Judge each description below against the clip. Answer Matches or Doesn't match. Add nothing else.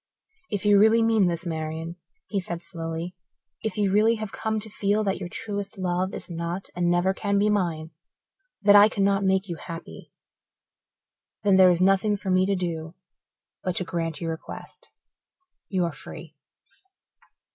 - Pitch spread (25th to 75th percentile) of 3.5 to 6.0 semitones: Doesn't match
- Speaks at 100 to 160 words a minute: Doesn't match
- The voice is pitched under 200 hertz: Matches